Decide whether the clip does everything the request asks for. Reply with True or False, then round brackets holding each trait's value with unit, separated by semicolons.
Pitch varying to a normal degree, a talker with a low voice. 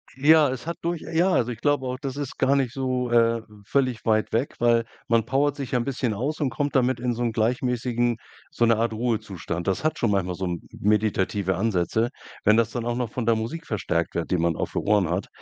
True (3.6 semitones; 120 Hz)